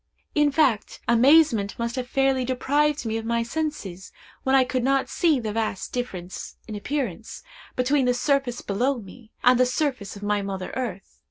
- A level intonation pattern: No, average, 3.9 semitones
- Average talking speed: Yes, average, 175 wpm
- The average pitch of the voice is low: No, very high, 250 Hz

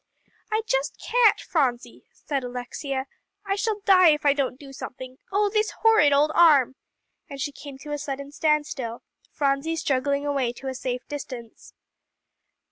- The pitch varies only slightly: No, average, 3.4 semitones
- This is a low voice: No, very high, 285 Hz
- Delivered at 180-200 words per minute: No, average, 155 wpm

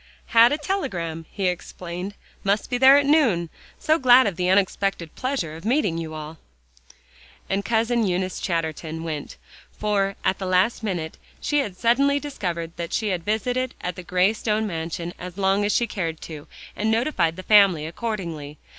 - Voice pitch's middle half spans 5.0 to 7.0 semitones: Yes, wide, 5.4 semitones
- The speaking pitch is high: Yes, high, 195 Hz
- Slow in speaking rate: No, average, 170 wpm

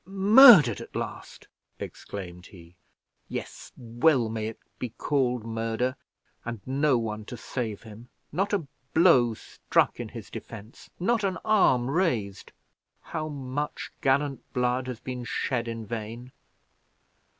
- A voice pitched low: Yes, low, 125 Hz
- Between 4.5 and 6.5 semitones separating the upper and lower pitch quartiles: Yes, average, 4.8 semitones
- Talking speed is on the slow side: Yes, slow, 130 wpm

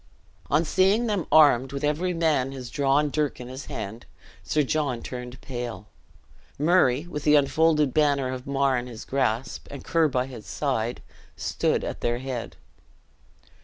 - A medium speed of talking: Yes, average, 160 wpm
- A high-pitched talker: No, low, 135 Hz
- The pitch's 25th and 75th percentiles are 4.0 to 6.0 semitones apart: No, average, 3.3 semitones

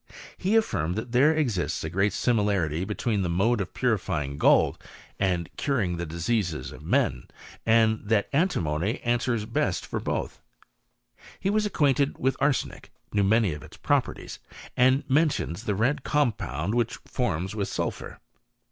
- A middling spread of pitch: No, wide, 6.5 semitones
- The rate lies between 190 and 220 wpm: No, average, 150 wpm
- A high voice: No, low, 110 Hz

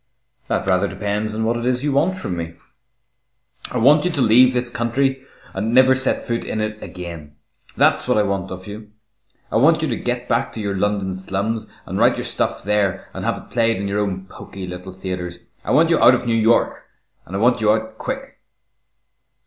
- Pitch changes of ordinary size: Yes, average, 4.3 semitones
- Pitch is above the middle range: No, low, 110 Hz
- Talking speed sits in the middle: No, fast, 215 wpm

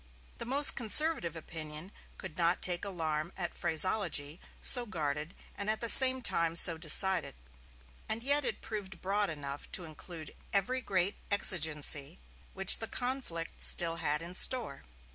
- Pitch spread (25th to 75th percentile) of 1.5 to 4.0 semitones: No, average, 5.0 semitones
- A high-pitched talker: No, medium, 180 Hz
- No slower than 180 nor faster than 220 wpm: No, average, 145 wpm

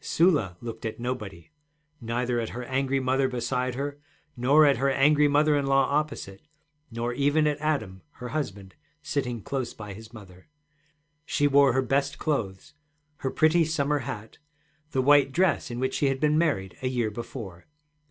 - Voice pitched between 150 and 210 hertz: No, low, 130 Hz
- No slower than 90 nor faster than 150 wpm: No, average, 170 wpm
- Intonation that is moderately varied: Yes, average, 3.6 semitones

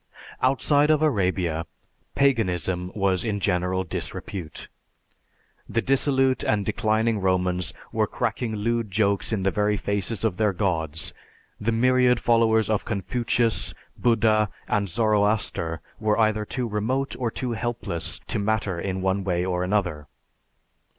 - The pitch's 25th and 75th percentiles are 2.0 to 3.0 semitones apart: No, average, 3.8 semitones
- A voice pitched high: No, low, 105 Hz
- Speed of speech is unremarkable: No, slow, 130 wpm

